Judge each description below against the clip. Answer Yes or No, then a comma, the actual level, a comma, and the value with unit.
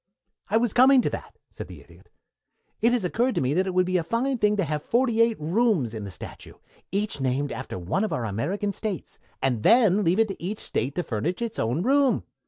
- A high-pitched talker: Yes, high, 195 Hz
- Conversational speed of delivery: No, fast, 230 wpm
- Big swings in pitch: Yes, wide, 8.1 semitones